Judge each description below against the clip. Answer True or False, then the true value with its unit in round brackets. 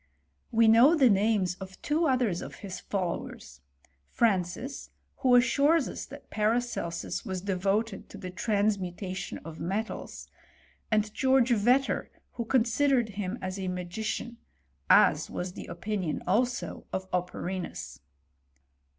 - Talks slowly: True (130 wpm)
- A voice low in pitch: False (210 Hz)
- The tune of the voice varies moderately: True (4.5 semitones)